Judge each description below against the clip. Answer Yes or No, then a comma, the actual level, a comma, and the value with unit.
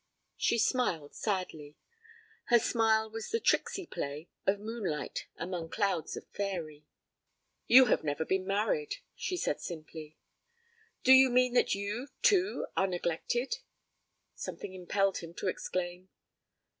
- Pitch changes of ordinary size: No, wide, 5.9 semitones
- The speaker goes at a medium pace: No, slow, 130 wpm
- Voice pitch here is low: No, high, 195 Hz